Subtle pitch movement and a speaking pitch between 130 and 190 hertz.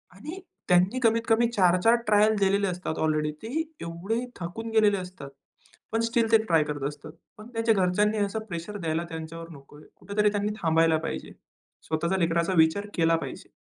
No: average, 4.8 semitones; medium, 185 Hz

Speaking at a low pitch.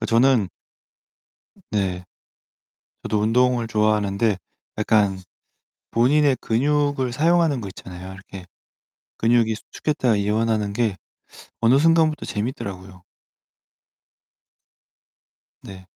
Yes: low, 110 Hz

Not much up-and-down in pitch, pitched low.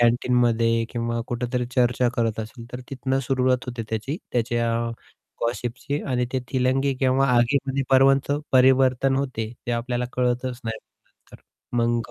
Yes: narrow, 1.9 semitones; low, 125 Hz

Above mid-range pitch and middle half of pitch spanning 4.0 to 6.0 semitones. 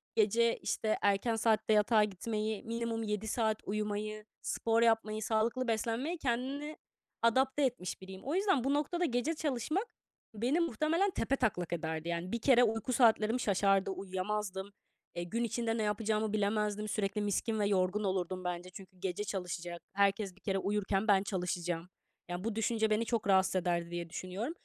No: high, 215 Hz; average, 3.3 semitones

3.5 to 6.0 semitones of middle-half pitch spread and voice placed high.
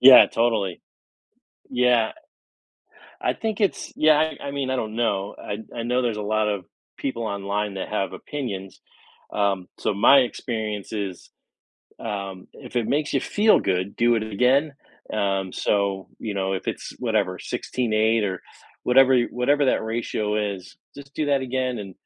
No: average, 4.2 semitones; low, 110 Hz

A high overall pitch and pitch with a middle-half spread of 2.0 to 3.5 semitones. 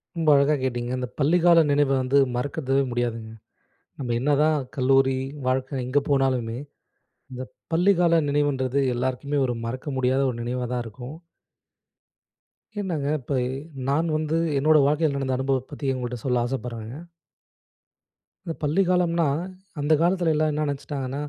No: low, 135 Hz; average, 3.2 semitones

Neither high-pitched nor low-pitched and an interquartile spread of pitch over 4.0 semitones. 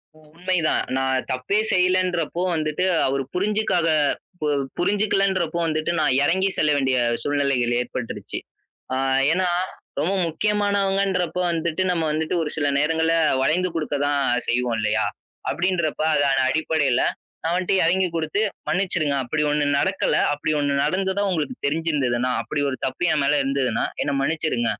Yes: medium, 160 Hz; average, 4.5 semitones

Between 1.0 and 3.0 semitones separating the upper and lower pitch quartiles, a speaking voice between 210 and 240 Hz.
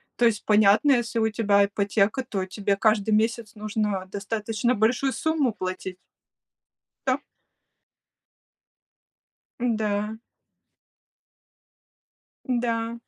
Yes: narrow, 2.4 semitones; high, 215 Hz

